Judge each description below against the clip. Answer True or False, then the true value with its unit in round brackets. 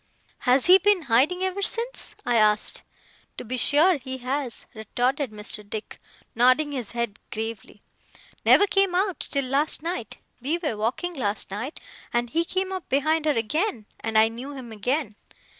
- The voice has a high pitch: True (260 Hz)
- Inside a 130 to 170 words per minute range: True (165 wpm)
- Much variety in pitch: True (6.5 semitones)